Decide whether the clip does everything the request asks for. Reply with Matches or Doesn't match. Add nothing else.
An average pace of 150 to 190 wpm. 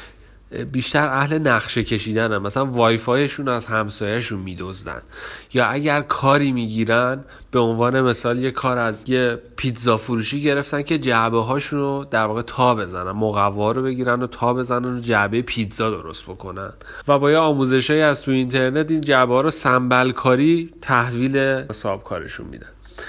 Matches